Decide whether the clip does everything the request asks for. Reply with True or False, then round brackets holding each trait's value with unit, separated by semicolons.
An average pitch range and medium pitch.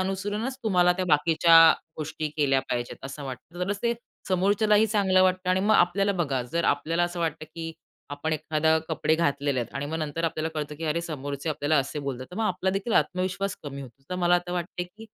True (4.0 semitones; 170 Hz)